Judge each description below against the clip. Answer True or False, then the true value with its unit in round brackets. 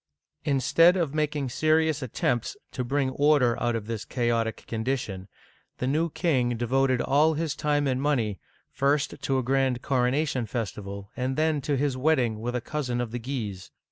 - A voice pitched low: True (130 Hz)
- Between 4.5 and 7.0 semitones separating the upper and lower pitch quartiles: False (3.6 semitones)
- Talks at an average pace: True (170 wpm)